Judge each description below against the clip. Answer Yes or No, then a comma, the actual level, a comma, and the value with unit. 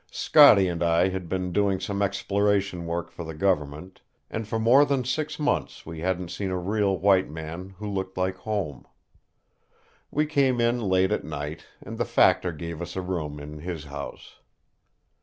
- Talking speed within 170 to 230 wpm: Yes, average, 175 wpm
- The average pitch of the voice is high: No, very low, 95 Hz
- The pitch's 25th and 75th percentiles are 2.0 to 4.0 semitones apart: Yes, average, 3.5 semitones